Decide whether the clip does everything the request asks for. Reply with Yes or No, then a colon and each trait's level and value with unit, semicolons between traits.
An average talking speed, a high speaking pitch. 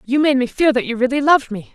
No: fast, 310 wpm; very high, 260 Hz